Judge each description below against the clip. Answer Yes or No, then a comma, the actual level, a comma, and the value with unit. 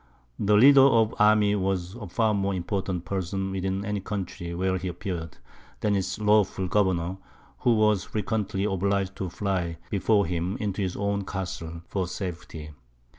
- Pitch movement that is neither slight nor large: No, narrow, 2.3 semitones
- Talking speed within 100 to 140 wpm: No, average, 160 wpm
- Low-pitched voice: Yes, very low, 95 Hz